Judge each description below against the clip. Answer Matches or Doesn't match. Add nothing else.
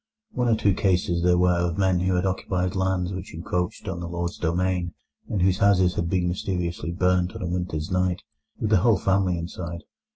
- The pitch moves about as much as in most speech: Doesn't match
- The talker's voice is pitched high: Doesn't match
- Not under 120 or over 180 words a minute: Doesn't match